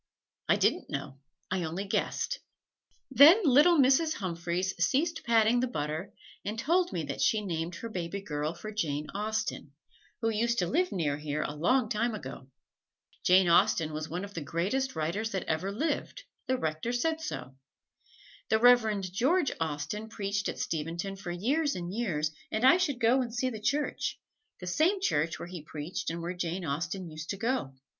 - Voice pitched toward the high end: Yes, high, 200 Hz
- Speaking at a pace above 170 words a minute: Yes, average, 180 wpm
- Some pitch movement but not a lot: No, wide, 6.7 semitones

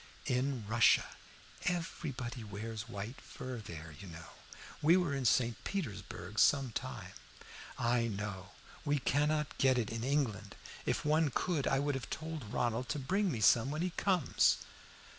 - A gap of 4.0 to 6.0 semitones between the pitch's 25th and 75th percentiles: Yes, wide, 5.4 semitones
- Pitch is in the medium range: No, low, 125 Hz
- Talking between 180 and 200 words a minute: No, average, 155 wpm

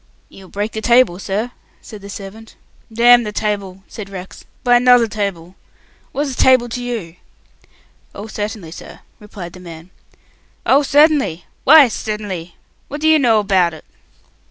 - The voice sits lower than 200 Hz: No, high, 210 Hz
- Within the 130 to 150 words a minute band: Yes, average, 145 wpm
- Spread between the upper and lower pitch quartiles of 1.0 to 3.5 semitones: No, average, 4.3 semitones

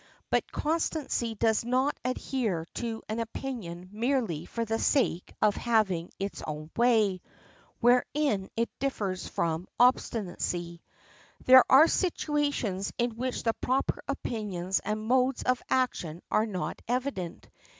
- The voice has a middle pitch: No, high, 225 Hz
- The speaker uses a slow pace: Yes, slow, 125 wpm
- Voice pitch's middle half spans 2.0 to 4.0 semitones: No, average, 5.1 semitones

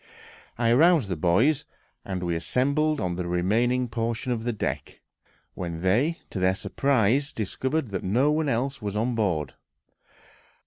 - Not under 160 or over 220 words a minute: No, average, 150 wpm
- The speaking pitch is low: Yes, low, 115 Hz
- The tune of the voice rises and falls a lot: Yes, wide, 6.4 semitones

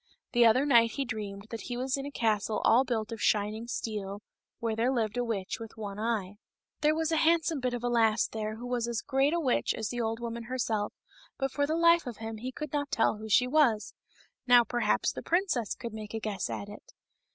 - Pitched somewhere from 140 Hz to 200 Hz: No, high, 235 Hz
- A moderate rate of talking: No, fast, 230 wpm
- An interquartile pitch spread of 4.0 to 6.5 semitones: No, average, 3.2 semitones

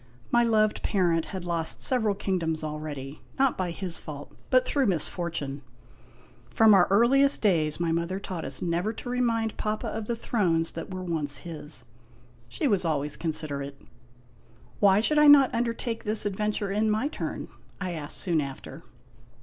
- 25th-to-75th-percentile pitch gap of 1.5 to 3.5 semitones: No, wide, 5.5 semitones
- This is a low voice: No, medium, 185 Hz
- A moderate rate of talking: Yes, average, 165 wpm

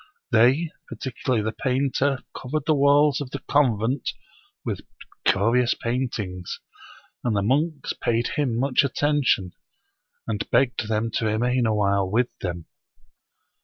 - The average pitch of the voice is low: Yes, low, 125 Hz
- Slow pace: Yes, slow, 130 wpm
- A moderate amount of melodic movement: Yes, average, 4.1 semitones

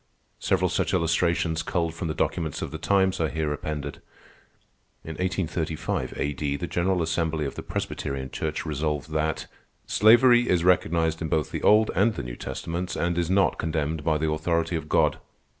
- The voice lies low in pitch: Yes, very low, 80 Hz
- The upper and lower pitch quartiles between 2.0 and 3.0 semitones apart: Yes, narrow, 2.5 semitones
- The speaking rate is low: No, average, 175 wpm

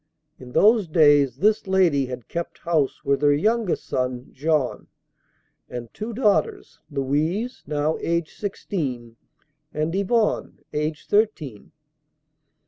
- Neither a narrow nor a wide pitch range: No, wide, 6.2 semitones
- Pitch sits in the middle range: Yes, medium, 155 Hz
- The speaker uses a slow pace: Yes, slow, 115 wpm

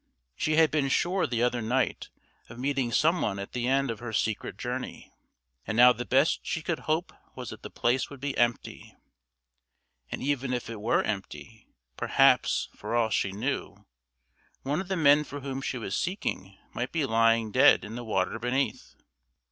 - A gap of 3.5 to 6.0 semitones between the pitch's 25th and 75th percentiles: Yes, average, 3.9 semitones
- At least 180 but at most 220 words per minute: Yes, average, 185 wpm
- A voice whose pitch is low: Yes, low, 125 Hz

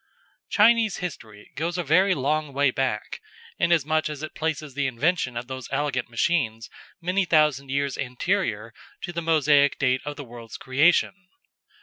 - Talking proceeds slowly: No, average, 150 wpm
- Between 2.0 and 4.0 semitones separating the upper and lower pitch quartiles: No, average, 4.7 semitones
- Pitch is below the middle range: No, medium, 145 Hz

